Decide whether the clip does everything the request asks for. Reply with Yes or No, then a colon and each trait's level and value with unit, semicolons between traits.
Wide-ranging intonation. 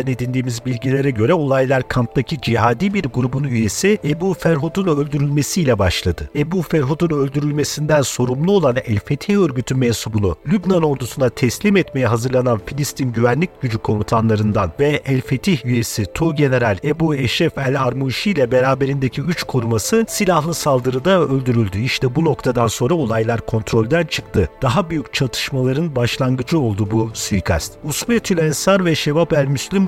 No: average, 4.7 semitones